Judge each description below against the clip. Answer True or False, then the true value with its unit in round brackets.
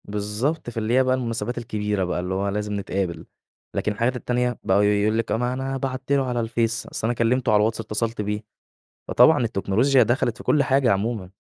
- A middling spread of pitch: True (3.0 semitones)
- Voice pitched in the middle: False (115 Hz)